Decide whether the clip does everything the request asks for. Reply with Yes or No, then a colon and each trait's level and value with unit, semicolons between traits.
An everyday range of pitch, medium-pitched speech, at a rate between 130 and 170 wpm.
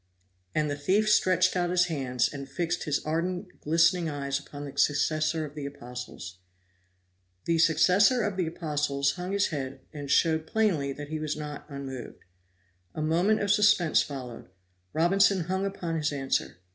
Yes: average, 4.2 semitones; medium, 155 Hz; average, 160 wpm